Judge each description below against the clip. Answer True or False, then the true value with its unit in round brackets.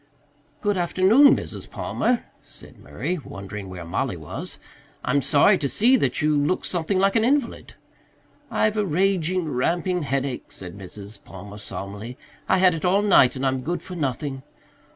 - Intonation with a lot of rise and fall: True (7.2 semitones)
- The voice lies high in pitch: False (160 Hz)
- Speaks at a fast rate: False (160 wpm)